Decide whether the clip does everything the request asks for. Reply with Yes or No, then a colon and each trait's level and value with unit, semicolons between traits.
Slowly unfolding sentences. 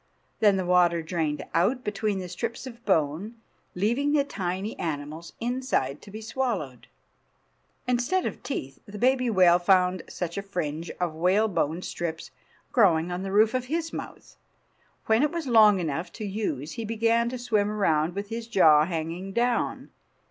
No: average, 160 wpm